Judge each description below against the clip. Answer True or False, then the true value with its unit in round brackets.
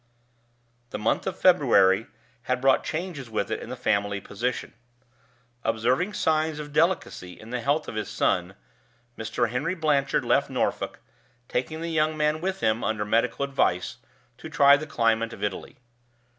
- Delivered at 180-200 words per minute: False (155 wpm)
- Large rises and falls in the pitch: True (5.8 semitones)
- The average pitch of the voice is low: True (125 Hz)